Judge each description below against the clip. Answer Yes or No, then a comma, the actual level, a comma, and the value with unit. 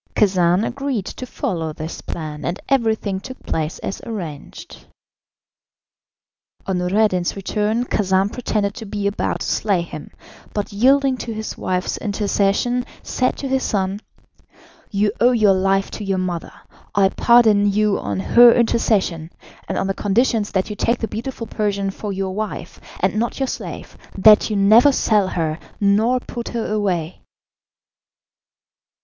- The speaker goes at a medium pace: Yes, average, 150 wpm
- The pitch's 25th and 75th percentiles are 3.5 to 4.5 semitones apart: No, average, 3.1 semitones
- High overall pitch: Yes, high, 205 Hz